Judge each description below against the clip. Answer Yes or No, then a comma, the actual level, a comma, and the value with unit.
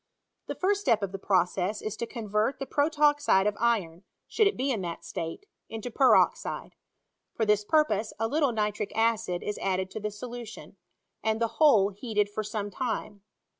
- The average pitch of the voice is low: No, high, 220 Hz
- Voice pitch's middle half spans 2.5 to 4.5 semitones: Yes, average, 3.7 semitones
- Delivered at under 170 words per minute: No, average, 180 wpm